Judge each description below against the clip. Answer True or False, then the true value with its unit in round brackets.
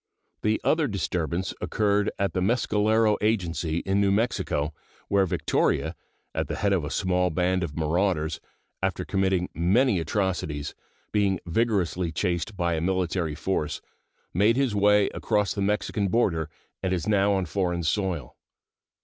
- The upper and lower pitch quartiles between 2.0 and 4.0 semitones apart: True (3.2 semitones)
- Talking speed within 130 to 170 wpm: True (145 wpm)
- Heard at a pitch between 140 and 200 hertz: False (95 Hz)